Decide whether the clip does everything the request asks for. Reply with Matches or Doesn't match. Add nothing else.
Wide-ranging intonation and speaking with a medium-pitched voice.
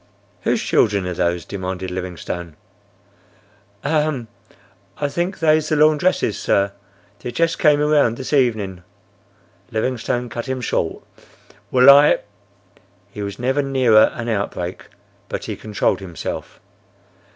Doesn't match